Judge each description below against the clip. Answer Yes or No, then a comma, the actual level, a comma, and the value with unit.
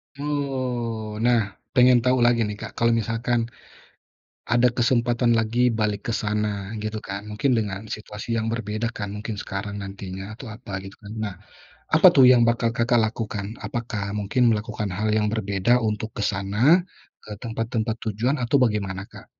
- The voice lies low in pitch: Yes, low, 110 Hz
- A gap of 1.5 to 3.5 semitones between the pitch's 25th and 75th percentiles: Yes, narrow, 2.4 semitones